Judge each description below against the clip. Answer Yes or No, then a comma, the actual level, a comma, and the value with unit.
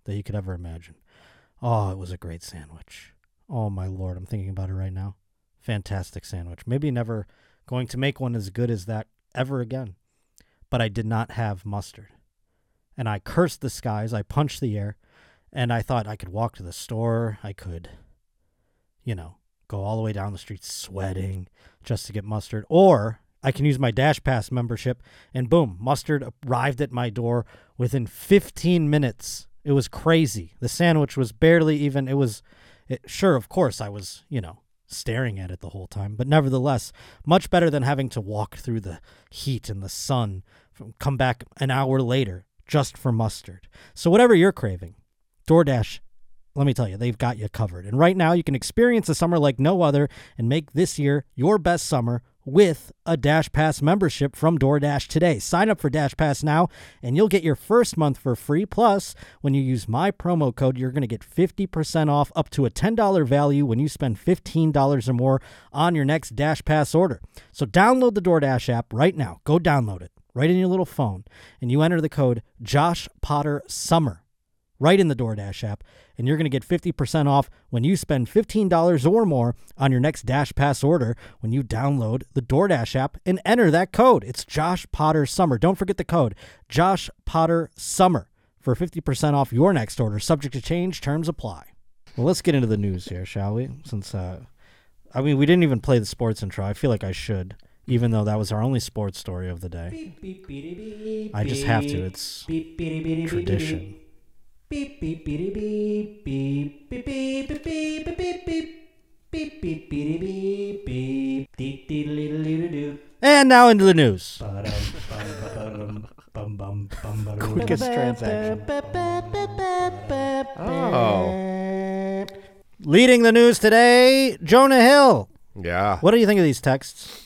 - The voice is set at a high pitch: No, low, 135 Hz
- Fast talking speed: No, average, 170 wpm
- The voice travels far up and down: Yes, wide, 7.3 semitones